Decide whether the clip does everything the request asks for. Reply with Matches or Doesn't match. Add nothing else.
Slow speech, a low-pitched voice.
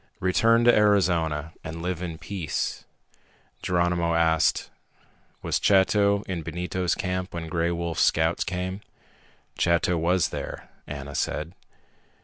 Matches